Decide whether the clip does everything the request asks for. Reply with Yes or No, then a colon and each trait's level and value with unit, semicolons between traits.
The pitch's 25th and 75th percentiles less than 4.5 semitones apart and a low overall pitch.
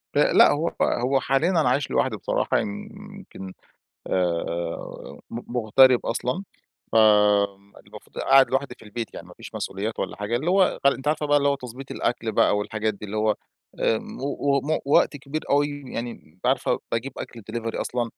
No: average, 4.9 semitones; low, 125 Hz